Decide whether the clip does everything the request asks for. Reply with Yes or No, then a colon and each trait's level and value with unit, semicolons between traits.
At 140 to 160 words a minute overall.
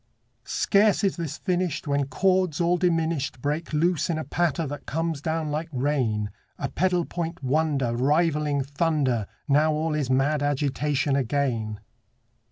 Yes: average, 145 wpm